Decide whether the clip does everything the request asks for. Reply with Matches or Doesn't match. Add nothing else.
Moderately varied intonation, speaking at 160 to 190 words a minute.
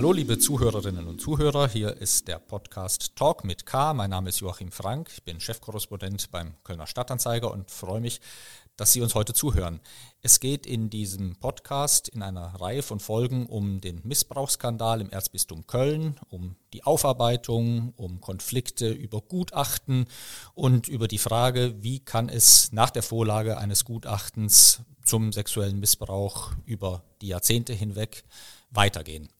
Doesn't match